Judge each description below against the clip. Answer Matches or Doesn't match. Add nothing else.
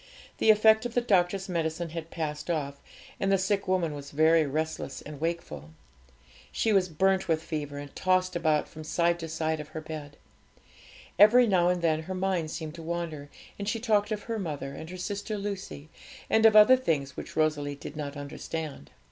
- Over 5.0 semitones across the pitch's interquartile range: Doesn't match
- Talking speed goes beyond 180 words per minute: Matches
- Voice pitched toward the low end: Doesn't match